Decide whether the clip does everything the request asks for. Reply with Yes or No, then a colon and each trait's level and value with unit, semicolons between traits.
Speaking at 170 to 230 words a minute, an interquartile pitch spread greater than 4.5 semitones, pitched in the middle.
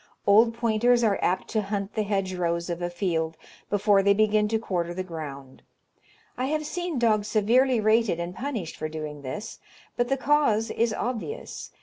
No: average, 175 wpm; average, 5.0 semitones; high, 210 Hz